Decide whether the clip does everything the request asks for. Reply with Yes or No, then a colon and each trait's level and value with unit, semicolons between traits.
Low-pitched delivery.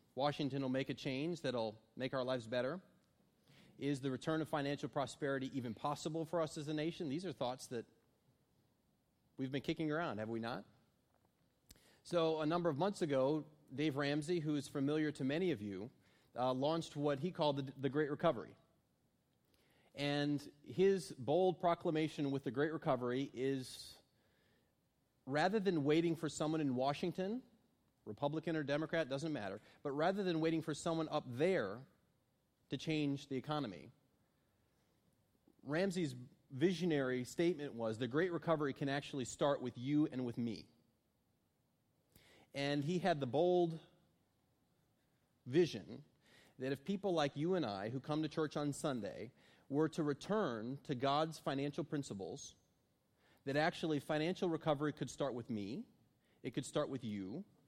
No: medium, 150 Hz